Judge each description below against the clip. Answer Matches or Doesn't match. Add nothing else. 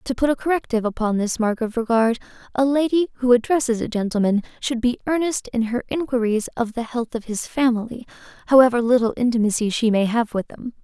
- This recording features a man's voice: Doesn't match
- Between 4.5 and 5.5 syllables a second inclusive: Doesn't match